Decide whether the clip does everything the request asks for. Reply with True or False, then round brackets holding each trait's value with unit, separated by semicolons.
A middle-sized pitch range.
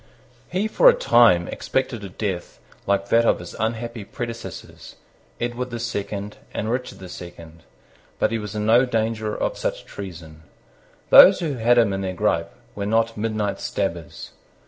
True (3.4 semitones)